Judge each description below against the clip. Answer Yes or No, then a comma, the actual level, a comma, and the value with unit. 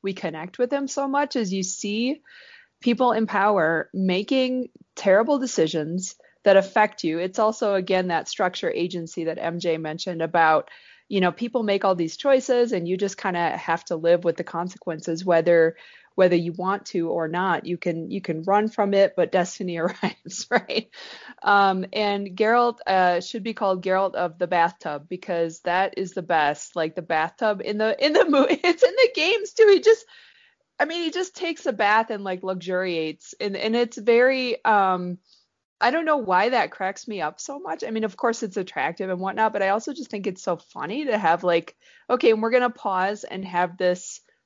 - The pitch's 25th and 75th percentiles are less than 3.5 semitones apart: No, wide, 5.4 semitones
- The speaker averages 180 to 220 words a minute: Yes, average, 195 wpm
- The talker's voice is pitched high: Yes, high, 195 Hz